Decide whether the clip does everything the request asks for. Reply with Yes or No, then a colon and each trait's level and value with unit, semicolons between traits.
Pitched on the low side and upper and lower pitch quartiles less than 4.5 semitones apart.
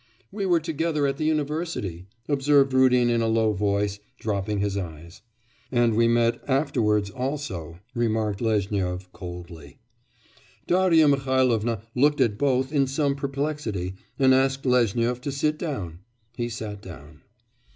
No: low, 120 Hz; wide, 5.5 semitones